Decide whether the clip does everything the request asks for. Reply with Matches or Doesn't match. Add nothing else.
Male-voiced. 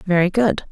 Doesn't match